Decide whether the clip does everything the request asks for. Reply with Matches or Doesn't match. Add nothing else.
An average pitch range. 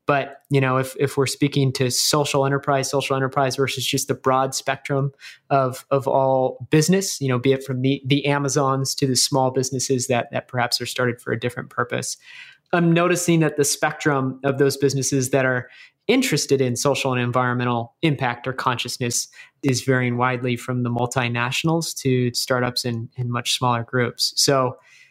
Doesn't match